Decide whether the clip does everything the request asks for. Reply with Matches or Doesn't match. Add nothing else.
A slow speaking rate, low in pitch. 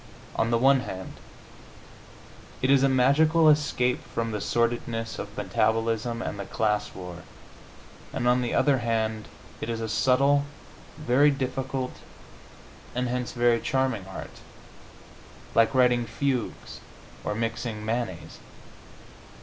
Matches